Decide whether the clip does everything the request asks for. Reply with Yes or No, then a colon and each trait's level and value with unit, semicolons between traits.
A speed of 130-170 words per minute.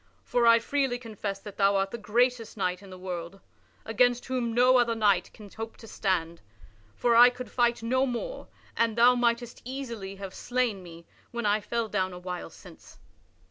No: average, 185 wpm